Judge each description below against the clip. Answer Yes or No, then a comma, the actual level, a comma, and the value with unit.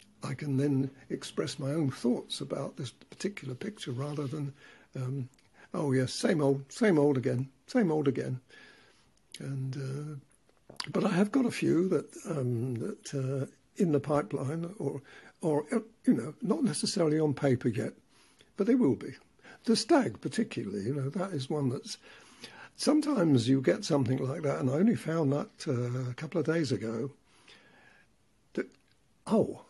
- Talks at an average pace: Yes, average, 160 wpm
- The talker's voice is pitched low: No, medium, 145 Hz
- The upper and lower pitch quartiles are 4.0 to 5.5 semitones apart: Yes, average, 5.2 semitones